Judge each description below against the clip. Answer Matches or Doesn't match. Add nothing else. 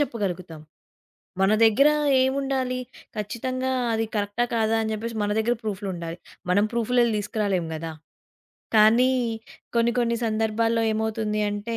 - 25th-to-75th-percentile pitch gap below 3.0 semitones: Matches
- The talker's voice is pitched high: Matches